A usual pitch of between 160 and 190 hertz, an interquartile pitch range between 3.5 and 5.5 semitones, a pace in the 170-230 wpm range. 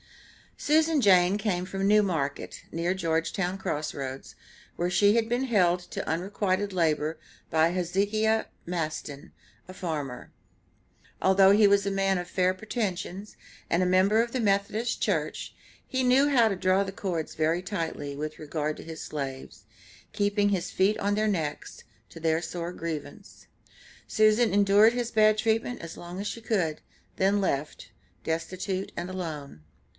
No: medium, 185 Hz; average, 3.9 semitones; average, 155 wpm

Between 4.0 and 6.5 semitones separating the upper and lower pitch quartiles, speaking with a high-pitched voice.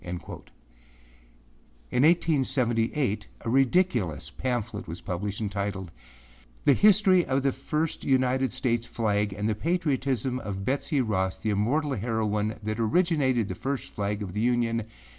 No: average, 4.7 semitones; low, 120 Hz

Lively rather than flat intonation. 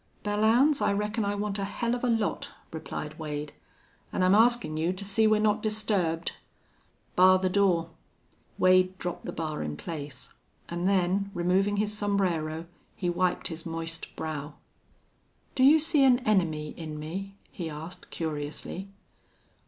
No: average, 4.3 semitones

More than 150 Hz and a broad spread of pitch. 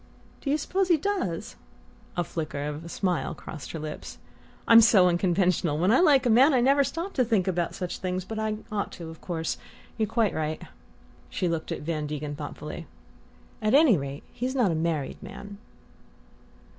Yes: medium, 185 Hz; wide, 7.0 semitones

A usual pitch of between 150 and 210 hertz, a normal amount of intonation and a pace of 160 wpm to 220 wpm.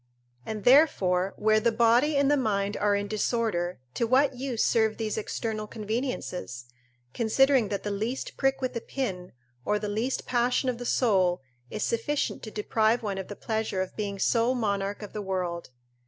No: high, 220 Hz; average, 3.4 semitones; average, 180 wpm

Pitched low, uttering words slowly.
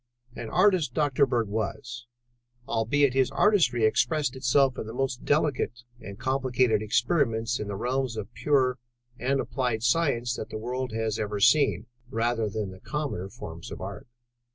No: low, 120 Hz; average, 160 wpm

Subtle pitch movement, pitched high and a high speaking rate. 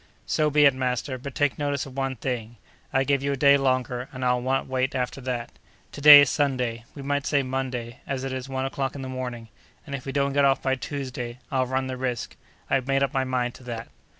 No: narrow, 1.6 semitones; low, 130 Hz; fast, 240 wpm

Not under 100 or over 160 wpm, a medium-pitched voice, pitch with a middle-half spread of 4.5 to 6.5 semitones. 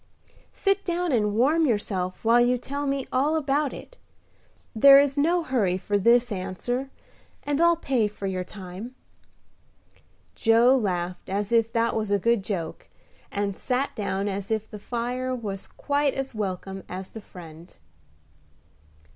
No: average, 150 wpm; high, 230 Hz; wide, 5.6 semitones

